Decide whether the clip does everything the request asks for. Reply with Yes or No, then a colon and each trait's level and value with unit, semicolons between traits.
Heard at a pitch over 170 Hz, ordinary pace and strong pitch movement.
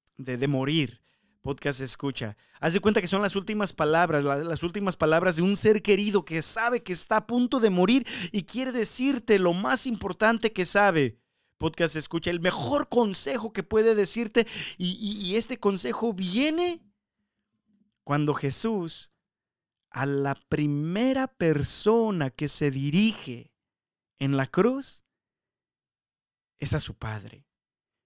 Yes: medium, 185 Hz; average, 140 wpm; wide, 7.1 semitones